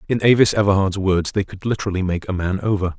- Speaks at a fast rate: Yes, fast, 220 wpm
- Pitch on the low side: Yes, very low, 95 Hz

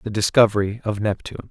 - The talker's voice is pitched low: Yes, low, 105 Hz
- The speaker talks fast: No, average, 160 wpm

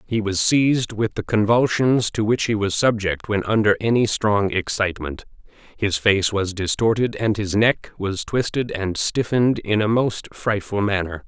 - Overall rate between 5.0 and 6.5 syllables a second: No, 4.6 syllables/s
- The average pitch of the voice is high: No, low, 105 Hz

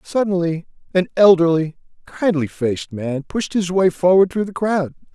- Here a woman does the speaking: No, male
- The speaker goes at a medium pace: Yes, average, 150 wpm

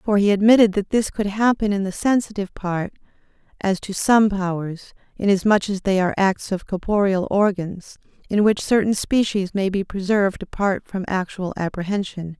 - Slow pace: No, average, 165 wpm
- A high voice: Yes, high, 200 Hz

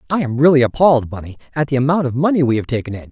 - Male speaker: Yes, male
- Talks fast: Yes, fast, 270 wpm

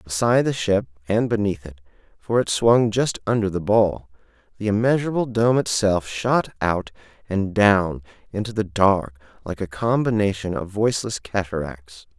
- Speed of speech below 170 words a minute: Yes, average, 150 wpm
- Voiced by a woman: No, male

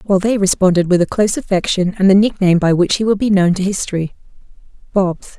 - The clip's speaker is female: Yes, female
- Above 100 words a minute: Yes, average, 200 wpm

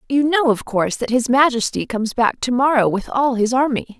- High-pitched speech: Yes, very high, 250 Hz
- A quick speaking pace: Yes, fast, 225 wpm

